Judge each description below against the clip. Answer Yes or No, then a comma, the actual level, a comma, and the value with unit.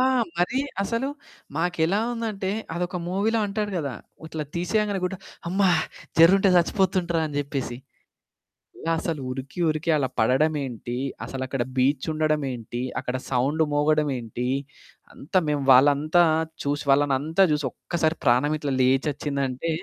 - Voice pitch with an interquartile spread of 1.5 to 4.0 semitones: No, average, 4.6 semitones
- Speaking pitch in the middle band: Yes, medium, 155 Hz